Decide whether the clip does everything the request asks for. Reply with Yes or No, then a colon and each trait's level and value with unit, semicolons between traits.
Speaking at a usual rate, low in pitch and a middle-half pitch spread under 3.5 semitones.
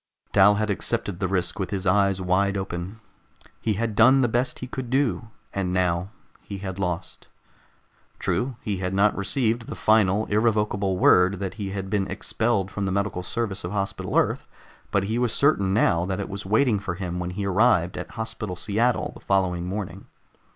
Yes: average, 185 wpm; low, 100 Hz; average, 2.8 semitones